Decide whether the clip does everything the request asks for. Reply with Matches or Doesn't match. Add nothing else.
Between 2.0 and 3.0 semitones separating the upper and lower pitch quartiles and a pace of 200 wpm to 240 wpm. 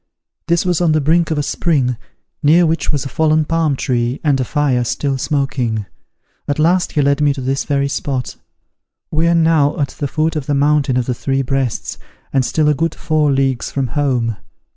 Matches